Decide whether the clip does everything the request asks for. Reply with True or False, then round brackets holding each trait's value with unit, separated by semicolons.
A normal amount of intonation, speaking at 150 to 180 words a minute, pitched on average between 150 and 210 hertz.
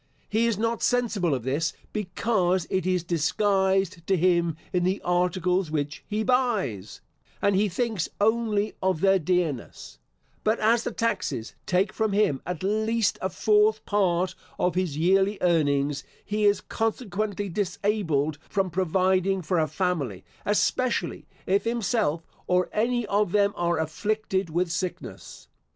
False (3.6 semitones; 140 wpm; 190 Hz)